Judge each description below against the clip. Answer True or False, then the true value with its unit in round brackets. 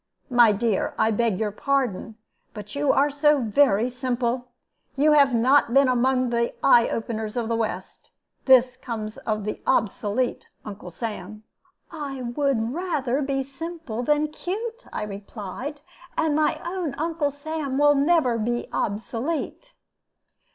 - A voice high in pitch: True (255 Hz)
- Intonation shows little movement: False (4.5 semitones)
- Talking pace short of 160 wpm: True (140 wpm)